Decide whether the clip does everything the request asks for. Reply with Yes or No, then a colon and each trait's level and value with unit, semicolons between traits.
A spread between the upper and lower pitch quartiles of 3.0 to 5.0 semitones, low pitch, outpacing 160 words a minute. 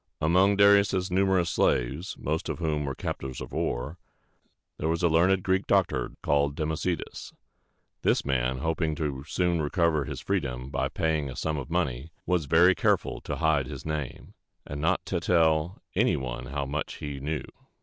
Yes: average, 3.8 semitones; very low, 80 Hz; average, 175 wpm